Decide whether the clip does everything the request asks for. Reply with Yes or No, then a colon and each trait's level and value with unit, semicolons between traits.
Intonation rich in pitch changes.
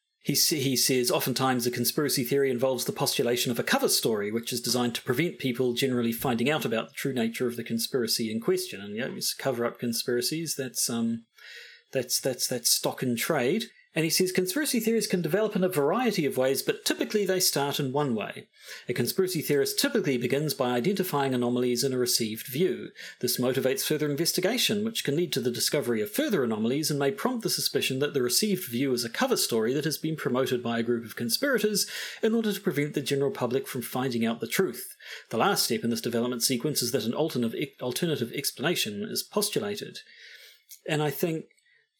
Yes: wide, 7.2 semitones